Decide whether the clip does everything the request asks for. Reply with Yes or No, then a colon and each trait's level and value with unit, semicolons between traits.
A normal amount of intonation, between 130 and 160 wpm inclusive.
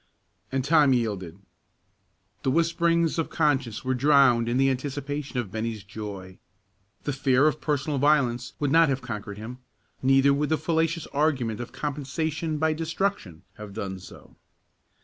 Yes: average, 4.6 semitones; average, 150 wpm